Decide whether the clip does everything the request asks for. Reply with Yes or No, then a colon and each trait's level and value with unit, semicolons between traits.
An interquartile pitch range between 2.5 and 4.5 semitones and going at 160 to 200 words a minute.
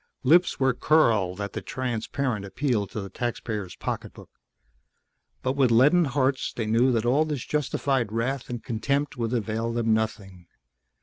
No: average, 3.7 semitones; average, 150 wpm